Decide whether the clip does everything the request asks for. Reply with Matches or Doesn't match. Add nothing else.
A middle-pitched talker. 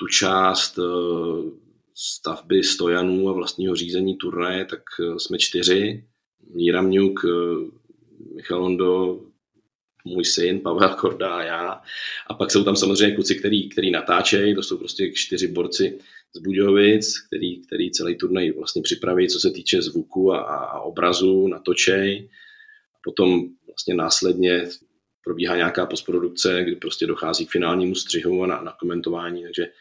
Doesn't match